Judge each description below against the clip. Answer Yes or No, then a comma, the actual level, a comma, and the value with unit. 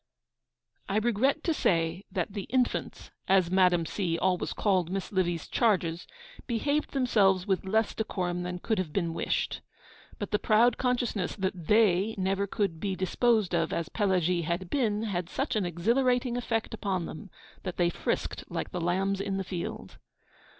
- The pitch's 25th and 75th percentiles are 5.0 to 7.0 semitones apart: No, average, 3.7 semitones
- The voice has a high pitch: Yes, high, 195 Hz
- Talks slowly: No, average, 165 wpm